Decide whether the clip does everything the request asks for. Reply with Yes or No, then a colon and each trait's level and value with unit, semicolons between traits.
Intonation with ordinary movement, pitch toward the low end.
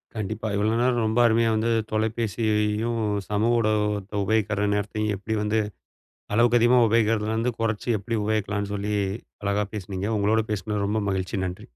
No: narrow, 1.6 semitones; low, 110 Hz